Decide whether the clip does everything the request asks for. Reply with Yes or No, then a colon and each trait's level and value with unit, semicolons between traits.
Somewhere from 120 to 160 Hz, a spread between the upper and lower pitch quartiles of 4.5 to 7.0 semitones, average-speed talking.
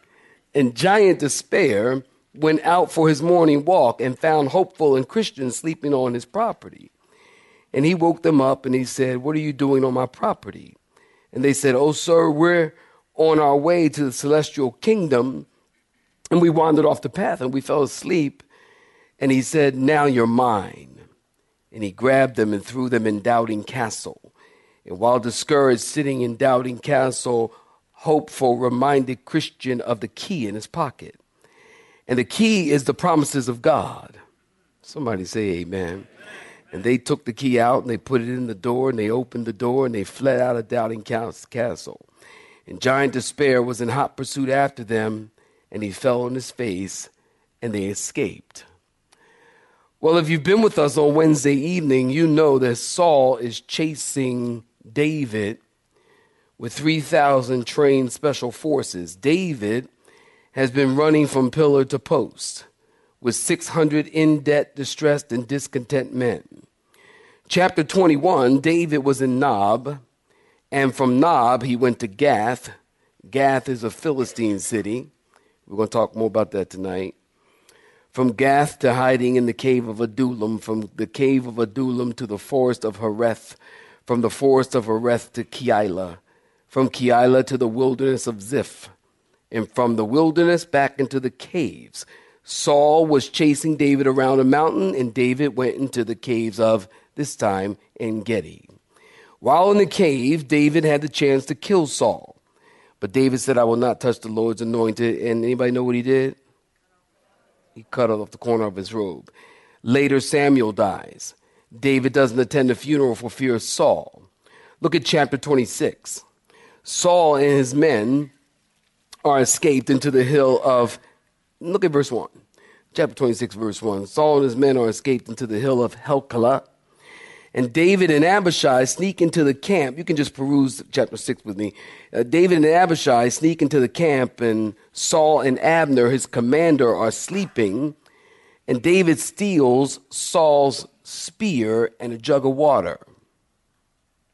No: low, 135 Hz; average, 4.1 semitones; average, 160 wpm